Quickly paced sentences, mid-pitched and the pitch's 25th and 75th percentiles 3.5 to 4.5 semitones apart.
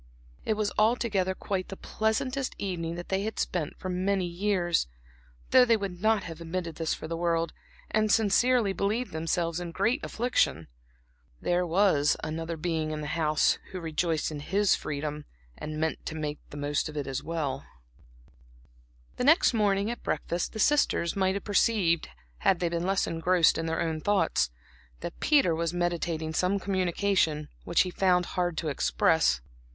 No: average, 165 wpm; medium, 175 Hz; average, 3.8 semitones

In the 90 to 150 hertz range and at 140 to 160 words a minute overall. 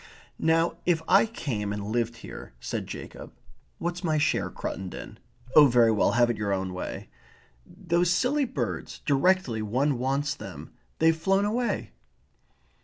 Yes: medium, 140 Hz; average, 150 wpm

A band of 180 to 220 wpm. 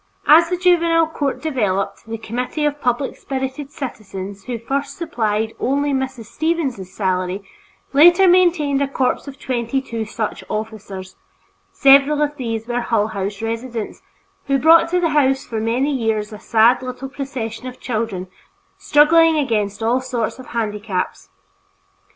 No: average, 145 wpm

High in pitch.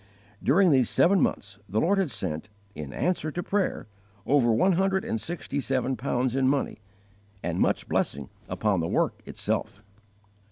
No: low, 130 Hz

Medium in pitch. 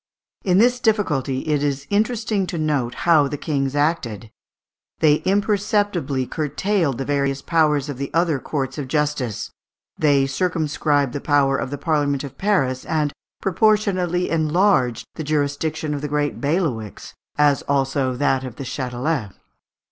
Yes: medium, 145 Hz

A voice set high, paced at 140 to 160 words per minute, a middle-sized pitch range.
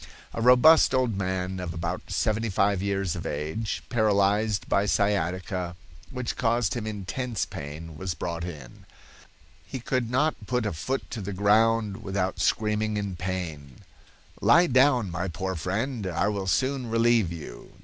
No: low, 100 Hz; average, 155 wpm; average, 4.0 semitones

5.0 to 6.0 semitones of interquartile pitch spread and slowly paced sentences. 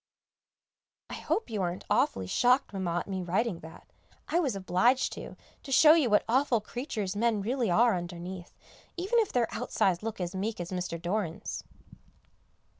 No: wide, 5.4 semitones; average, 165 wpm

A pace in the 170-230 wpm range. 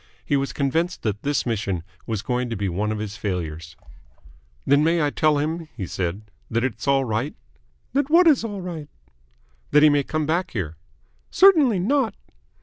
Yes: average, 180 wpm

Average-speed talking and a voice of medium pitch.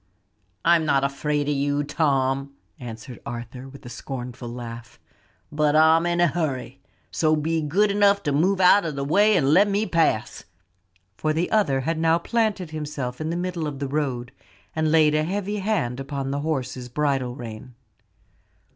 Yes: average, 175 wpm; medium, 150 Hz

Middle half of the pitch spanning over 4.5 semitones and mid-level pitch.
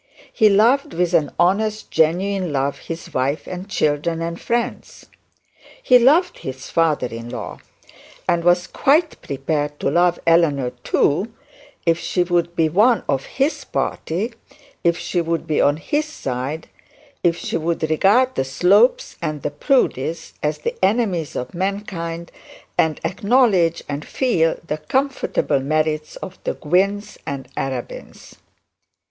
Yes: average, 4.9 semitones; medium, 170 Hz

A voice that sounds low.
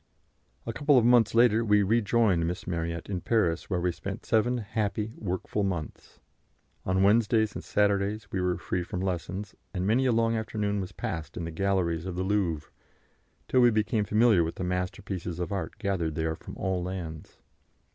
Yes: low, 100 Hz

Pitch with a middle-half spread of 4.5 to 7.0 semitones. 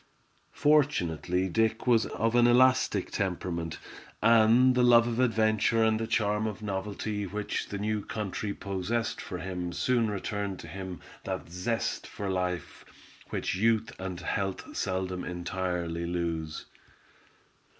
No: average, 3.8 semitones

